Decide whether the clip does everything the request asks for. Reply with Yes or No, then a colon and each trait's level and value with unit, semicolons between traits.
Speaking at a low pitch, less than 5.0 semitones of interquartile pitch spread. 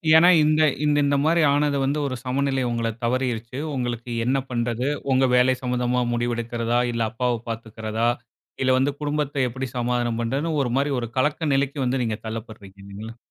Yes: low, 125 Hz; average, 2.9 semitones